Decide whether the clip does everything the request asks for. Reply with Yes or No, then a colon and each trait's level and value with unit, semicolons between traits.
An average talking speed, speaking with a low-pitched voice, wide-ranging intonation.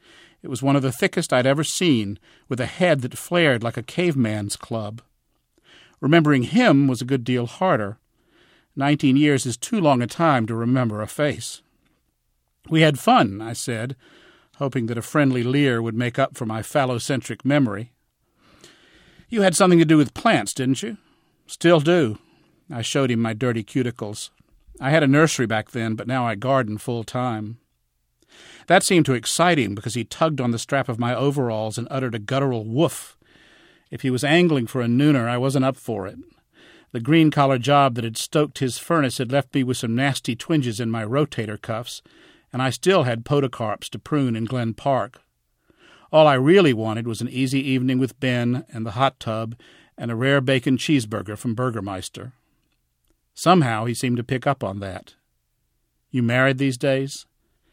No: average, 185 wpm; low, 130 Hz; average, 3.8 semitones